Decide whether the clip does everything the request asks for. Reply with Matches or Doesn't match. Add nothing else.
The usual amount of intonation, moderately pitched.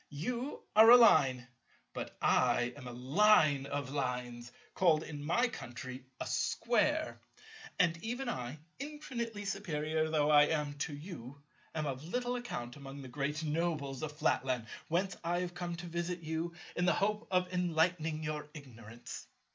Matches